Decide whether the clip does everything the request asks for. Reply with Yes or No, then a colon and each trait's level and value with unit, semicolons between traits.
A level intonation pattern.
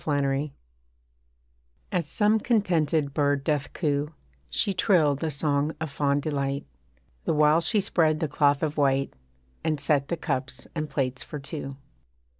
Yes: narrow, 2.2 semitones